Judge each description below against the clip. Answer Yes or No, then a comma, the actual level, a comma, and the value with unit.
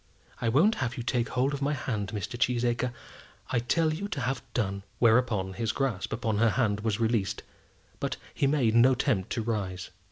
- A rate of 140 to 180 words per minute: No, average, 190 wpm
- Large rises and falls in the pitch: No, average, 3.4 semitones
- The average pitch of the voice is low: Yes, low, 120 Hz